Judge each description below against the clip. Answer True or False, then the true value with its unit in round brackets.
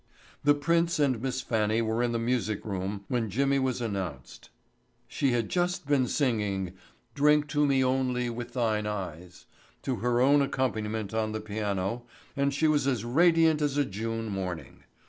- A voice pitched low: True (120 Hz)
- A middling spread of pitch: True (4.5 semitones)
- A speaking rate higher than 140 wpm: True (165 wpm)